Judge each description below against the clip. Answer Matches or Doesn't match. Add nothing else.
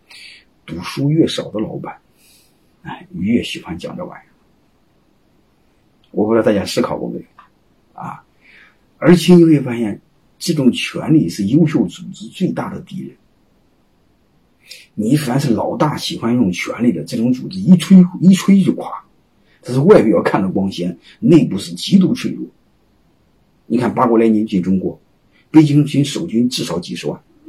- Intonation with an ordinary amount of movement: Doesn't match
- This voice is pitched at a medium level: Matches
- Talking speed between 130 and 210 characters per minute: Doesn't match